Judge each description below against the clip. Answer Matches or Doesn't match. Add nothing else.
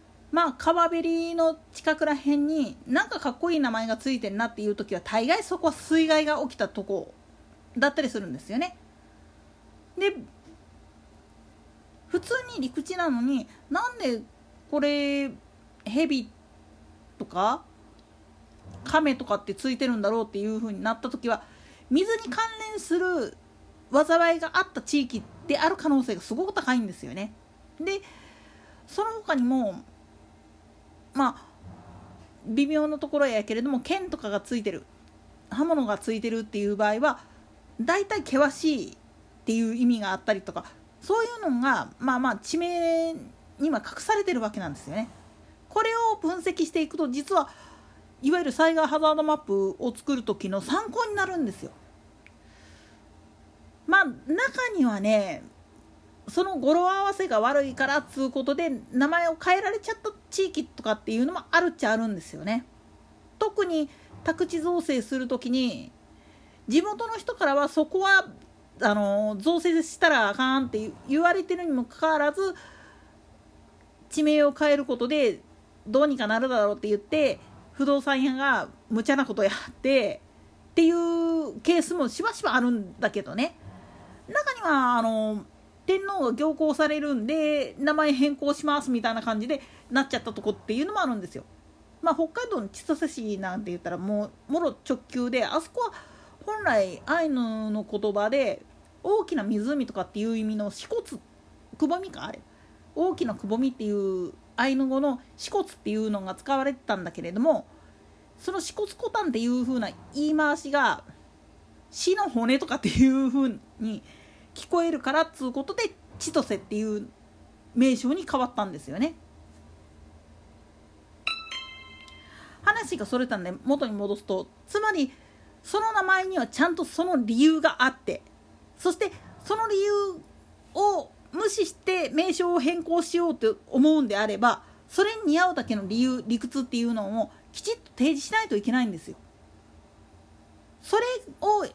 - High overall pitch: Matches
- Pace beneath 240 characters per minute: Doesn't match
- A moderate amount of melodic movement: Doesn't match